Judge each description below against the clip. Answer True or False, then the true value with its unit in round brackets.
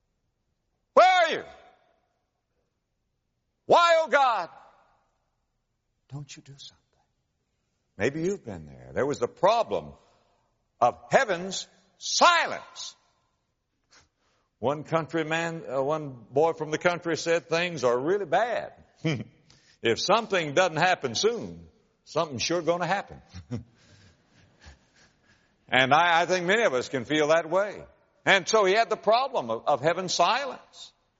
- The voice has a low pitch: False (165 Hz)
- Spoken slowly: True (120 wpm)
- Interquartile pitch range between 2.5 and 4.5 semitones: False (5.2 semitones)